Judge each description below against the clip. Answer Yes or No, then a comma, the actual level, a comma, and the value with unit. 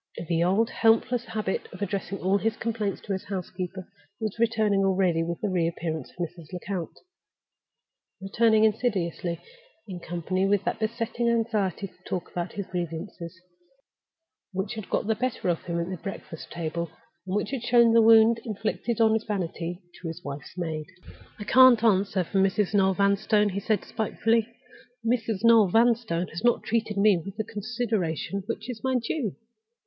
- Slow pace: No, average, 165 wpm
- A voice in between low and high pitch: No, high, 200 Hz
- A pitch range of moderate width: Yes, average, 3.9 semitones